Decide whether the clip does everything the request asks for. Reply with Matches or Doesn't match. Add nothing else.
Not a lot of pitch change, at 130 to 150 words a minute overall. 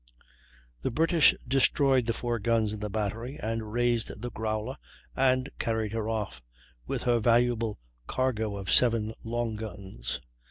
Matches